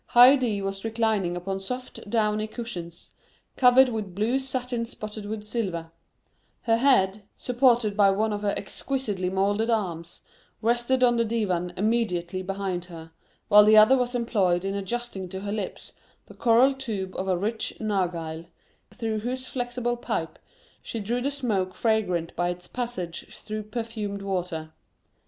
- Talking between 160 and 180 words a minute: No, average, 150 wpm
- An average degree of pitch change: Yes, average, 4.0 semitones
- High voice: Yes, high, 215 Hz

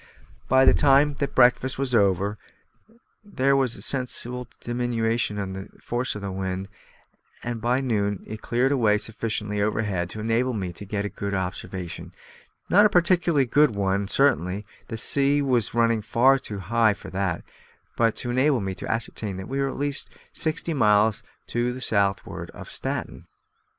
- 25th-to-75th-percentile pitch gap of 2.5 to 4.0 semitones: No, average, 4.6 semitones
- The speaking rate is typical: Yes, average, 165 wpm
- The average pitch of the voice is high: No, low, 115 Hz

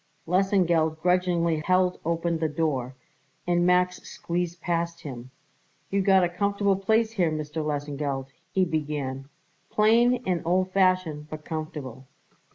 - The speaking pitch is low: No, medium, 170 Hz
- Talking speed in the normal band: No, slow, 130 wpm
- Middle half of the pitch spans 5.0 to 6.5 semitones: No, average, 3.3 semitones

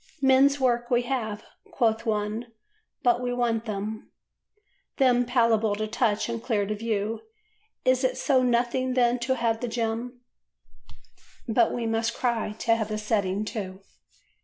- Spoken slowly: No, average, 150 wpm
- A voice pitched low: No, high, 230 Hz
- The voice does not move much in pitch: Yes, narrow, 2.2 semitones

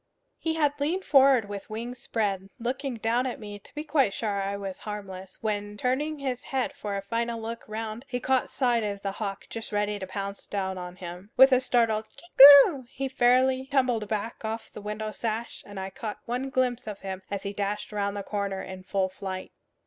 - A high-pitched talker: Yes, high, 220 Hz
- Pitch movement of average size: Yes, average, 4.2 semitones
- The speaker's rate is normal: No, fast, 210 wpm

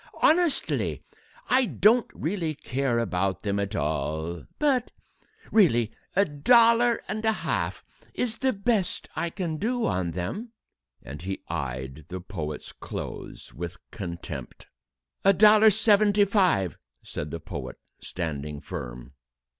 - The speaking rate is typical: No, slow, 125 wpm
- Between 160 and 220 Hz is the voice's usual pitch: No, low, 125 Hz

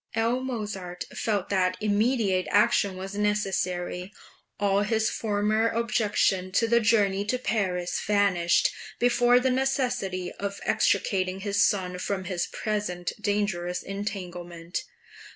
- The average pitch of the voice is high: Yes, high, 200 Hz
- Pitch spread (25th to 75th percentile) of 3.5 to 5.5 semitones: No, average, 2.9 semitones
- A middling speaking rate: No, slow, 115 wpm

